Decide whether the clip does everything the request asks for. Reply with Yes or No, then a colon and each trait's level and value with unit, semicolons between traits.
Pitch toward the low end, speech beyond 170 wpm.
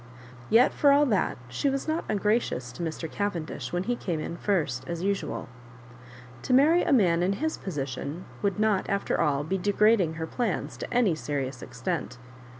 No: high, 190 Hz; average, 180 wpm